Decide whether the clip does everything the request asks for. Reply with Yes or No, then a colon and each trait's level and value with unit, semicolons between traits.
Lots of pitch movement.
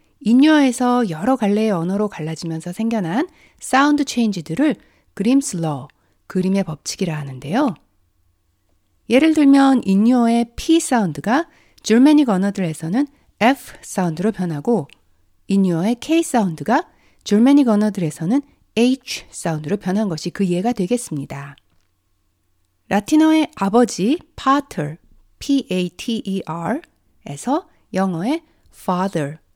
Yes: wide, 8.1 semitones